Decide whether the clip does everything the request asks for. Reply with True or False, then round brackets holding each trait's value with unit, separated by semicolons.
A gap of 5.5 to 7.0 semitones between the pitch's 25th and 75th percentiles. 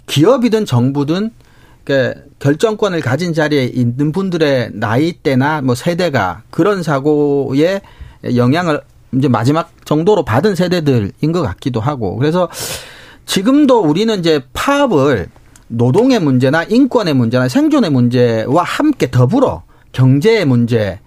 True (6.2 semitones)